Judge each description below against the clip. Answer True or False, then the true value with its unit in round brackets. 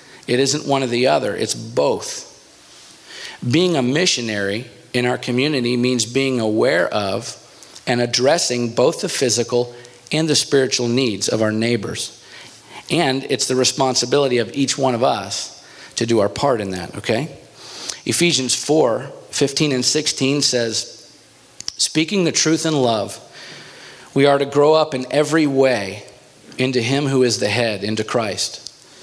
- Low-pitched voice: True (130 Hz)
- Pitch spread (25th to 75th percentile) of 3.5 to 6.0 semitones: False (2.8 semitones)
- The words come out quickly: False (150 wpm)